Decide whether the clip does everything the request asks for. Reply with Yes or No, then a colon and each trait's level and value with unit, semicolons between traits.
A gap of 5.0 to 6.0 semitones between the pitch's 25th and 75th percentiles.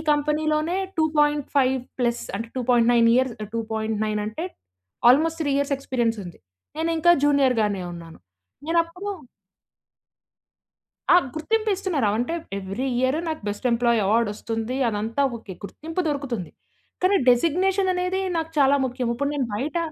Yes: wide, 5.6 semitones